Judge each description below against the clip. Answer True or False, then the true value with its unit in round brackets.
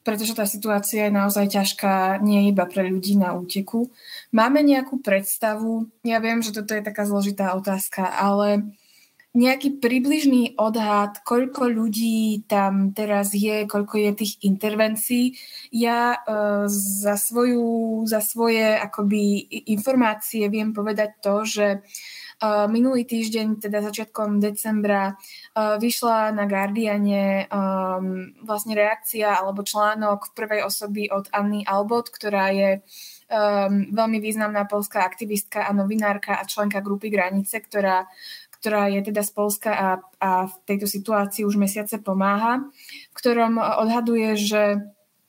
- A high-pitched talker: True (210 Hz)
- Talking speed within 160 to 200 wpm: False (125 wpm)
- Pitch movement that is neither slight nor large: False (1.9 semitones)